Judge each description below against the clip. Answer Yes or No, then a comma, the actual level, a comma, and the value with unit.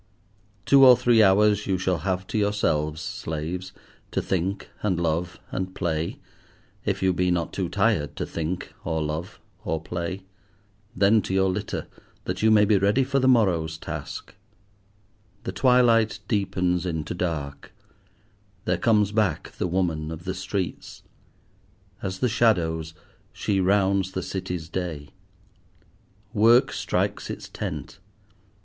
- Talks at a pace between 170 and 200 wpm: No, average, 140 wpm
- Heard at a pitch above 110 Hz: No, very low, 95 Hz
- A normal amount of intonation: Yes, average, 3.7 semitones